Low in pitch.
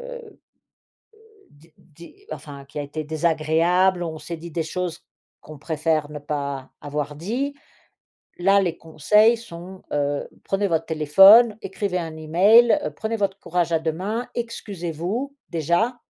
No: medium, 170 Hz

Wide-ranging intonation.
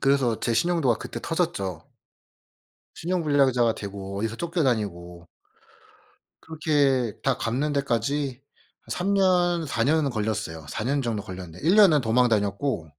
Yes: wide, 6.2 semitones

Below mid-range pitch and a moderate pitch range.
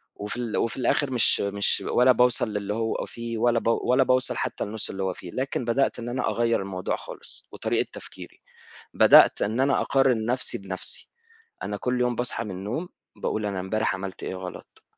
Yes: low, 115 Hz; average, 3.6 semitones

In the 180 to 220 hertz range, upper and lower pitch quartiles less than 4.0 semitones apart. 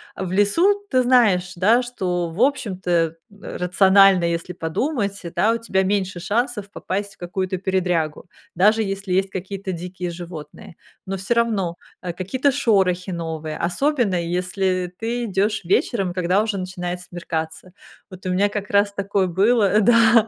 Yes: high, 190 Hz; average, 2.8 semitones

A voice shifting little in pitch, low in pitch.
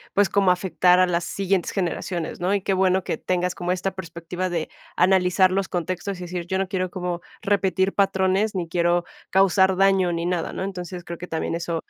No: narrow, 1.5 semitones; medium, 185 Hz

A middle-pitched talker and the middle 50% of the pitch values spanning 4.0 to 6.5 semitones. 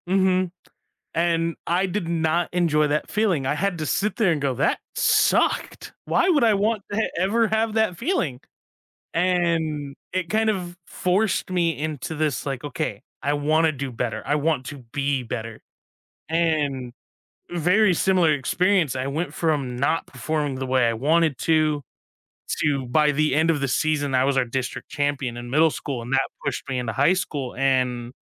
Yes: medium, 155 Hz; average, 4.6 semitones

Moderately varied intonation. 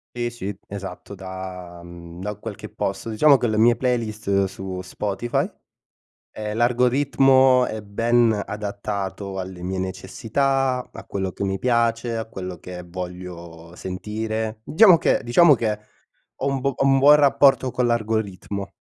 Yes: average, 4.5 semitones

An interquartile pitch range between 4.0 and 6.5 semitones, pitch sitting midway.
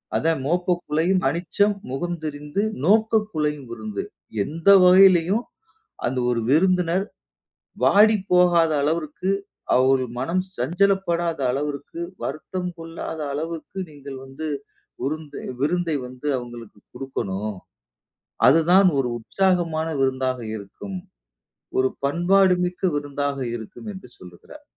Yes: average, 5.0 semitones; medium, 160 Hz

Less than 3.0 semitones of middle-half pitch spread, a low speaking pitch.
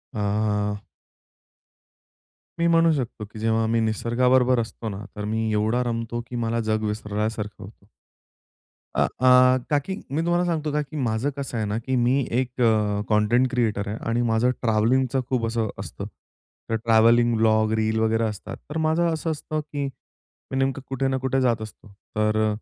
No: average, 3.3 semitones; low, 115 Hz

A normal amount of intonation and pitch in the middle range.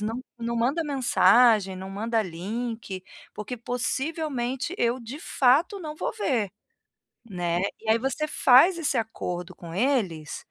No: average, 4.7 semitones; high, 235 Hz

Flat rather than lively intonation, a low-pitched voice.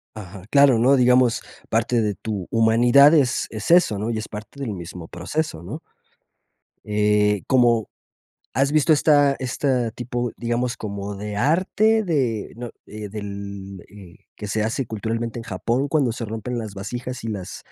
No: average, 3.7 semitones; low, 115 Hz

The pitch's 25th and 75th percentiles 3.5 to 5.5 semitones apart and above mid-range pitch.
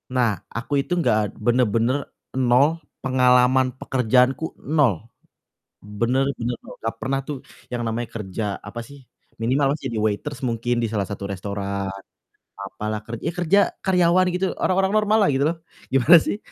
No: average, 4.0 semitones; low, 125 Hz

